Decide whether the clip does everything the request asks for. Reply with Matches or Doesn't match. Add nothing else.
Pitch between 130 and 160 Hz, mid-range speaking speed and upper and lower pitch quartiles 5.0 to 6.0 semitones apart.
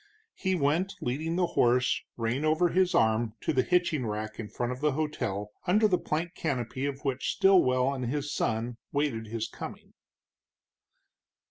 Matches